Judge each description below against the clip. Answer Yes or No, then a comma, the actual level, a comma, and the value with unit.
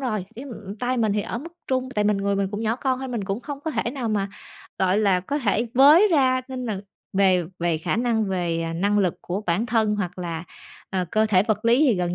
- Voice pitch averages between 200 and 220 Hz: Yes, high, 215 Hz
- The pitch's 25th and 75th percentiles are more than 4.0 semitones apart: Yes, average, 4.7 semitones